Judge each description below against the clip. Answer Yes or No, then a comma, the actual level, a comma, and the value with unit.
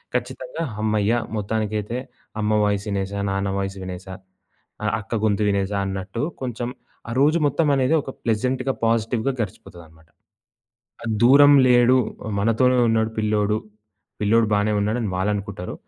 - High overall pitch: No, low, 110 Hz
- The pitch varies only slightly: No, average, 3.0 semitones